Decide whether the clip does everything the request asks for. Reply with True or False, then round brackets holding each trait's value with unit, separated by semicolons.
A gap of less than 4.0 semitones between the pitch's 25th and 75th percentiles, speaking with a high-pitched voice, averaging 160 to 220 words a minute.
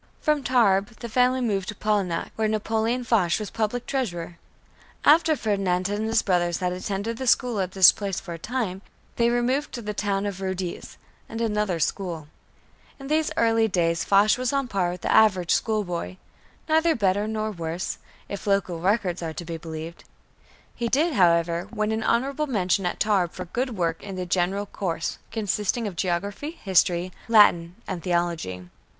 False (4.3 semitones; 200 Hz; 175 wpm)